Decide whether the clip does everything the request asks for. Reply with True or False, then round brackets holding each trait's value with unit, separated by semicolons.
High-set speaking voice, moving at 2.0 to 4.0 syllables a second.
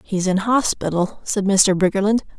False (195 Hz; 4.7 syllables/s)